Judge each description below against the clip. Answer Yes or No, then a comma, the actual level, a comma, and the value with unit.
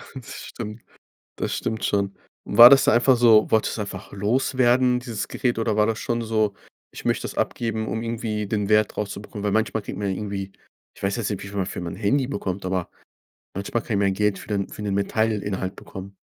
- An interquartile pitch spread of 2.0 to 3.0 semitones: Yes, narrow, 2.6 semitones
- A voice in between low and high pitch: No, low, 105 Hz